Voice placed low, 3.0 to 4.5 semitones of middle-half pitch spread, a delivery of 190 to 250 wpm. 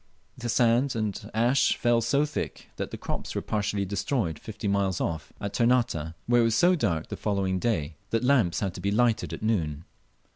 Yes: low, 110 Hz; average, 3.9 semitones; average, 195 wpm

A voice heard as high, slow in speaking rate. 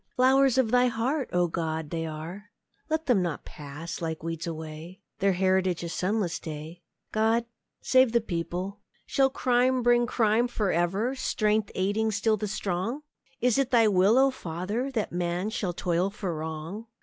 No: high, 200 Hz; average, 165 wpm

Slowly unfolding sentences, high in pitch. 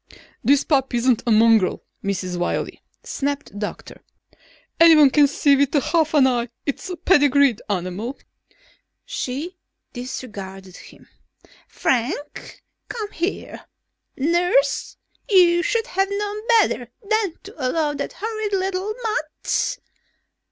Yes: slow, 115 wpm; very high, 290 Hz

